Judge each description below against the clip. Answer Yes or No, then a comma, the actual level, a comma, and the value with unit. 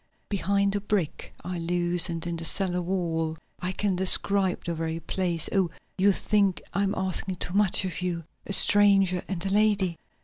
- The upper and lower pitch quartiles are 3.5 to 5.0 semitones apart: No, narrow, 2.4 semitones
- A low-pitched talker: No, medium, 185 Hz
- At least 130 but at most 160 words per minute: No, average, 175 wpm